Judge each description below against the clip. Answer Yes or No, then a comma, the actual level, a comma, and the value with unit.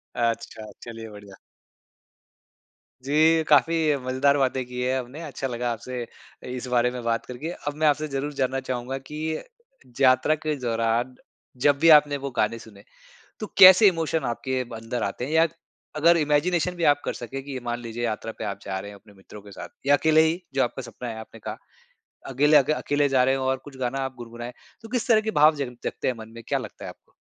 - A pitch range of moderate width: Yes, average, 4.0 semitones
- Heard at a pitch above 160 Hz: No, low, 130 Hz